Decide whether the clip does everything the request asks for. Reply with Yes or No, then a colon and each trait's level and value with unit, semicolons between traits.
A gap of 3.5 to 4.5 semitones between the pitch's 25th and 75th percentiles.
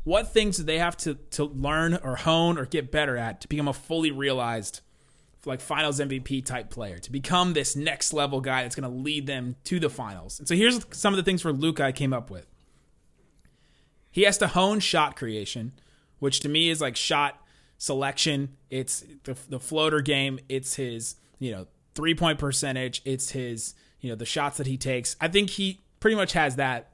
Yes: average, 3.8 semitones